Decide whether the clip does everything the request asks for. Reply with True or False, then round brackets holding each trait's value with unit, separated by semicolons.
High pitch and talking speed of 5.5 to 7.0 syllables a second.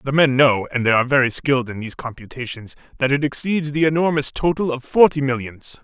False (135 Hz; 6.1 syllables/s)